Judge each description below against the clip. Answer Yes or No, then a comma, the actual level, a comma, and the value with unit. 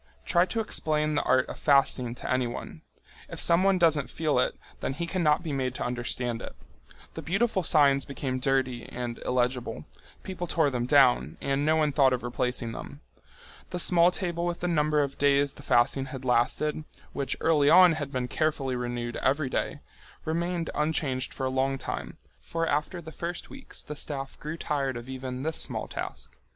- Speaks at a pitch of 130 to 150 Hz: Yes, medium, 140 Hz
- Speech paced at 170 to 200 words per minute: Yes, average, 185 wpm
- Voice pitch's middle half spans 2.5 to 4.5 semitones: Yes, average, 3.9 semitones